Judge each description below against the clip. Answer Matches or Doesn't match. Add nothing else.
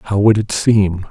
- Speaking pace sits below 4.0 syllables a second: Matches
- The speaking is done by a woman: Doesn't match